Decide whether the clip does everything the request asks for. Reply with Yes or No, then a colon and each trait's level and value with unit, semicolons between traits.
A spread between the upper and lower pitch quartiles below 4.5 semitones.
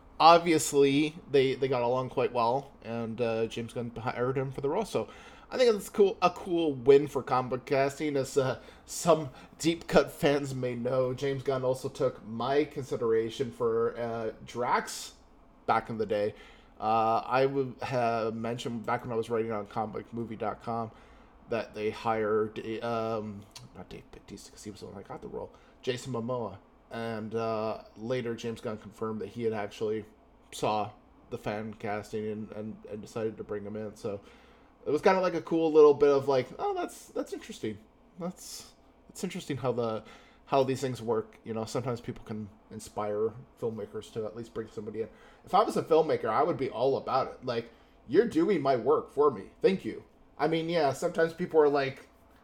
No: average, 4.9 semitones